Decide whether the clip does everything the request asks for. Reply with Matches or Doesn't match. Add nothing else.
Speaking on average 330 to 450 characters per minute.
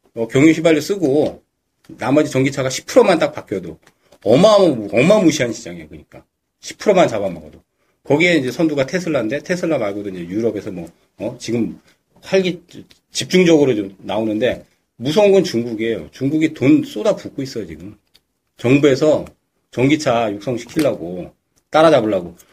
Matches